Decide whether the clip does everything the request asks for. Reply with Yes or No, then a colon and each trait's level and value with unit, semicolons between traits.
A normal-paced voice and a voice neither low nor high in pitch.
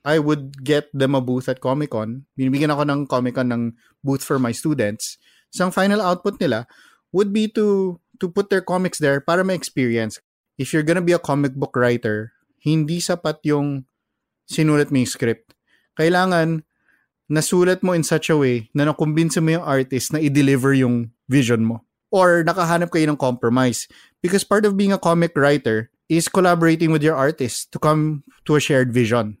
Yes: average, 180 wpm; medium, 150 Hz